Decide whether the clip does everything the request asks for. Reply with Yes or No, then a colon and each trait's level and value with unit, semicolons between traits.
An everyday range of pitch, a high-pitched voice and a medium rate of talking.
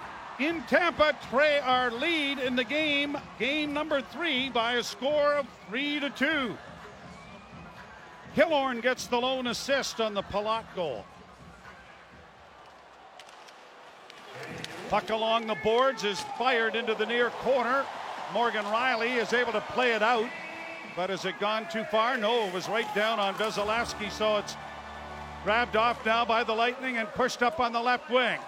Yes: average, 3.6 semitones; high, 235 Hz; average, 155 wpm